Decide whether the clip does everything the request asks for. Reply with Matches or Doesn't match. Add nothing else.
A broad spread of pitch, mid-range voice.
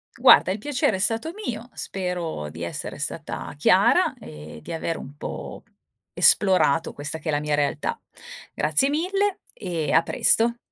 Matches